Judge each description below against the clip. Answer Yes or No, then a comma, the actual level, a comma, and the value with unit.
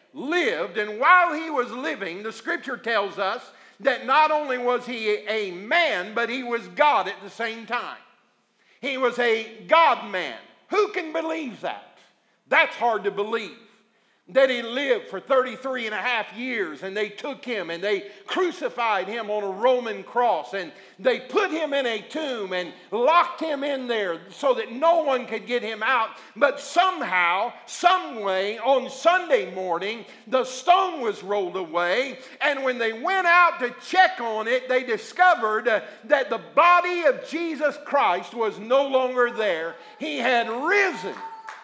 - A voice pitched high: Yes, very high, 255 Hz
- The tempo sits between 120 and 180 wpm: Yes, average, 165 wpm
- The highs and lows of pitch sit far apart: Yes, wide, 6.4 semitones